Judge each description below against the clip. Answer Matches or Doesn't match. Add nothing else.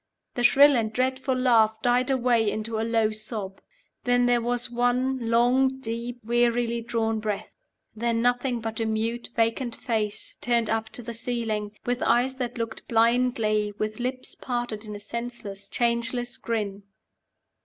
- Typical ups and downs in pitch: Doesn't match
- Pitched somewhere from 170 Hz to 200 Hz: Doesn't match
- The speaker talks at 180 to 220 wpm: Doesn't match